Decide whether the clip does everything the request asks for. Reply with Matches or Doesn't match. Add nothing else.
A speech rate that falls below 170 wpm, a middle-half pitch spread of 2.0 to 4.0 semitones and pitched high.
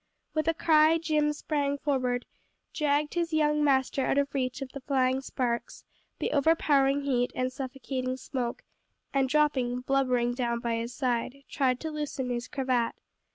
Matches